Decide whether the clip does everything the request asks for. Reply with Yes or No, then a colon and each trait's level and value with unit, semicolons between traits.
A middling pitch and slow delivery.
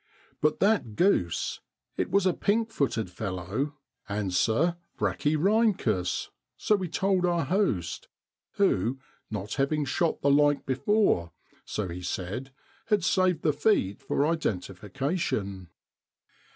Yes: medium, 145 Hz; slow, 115 wpm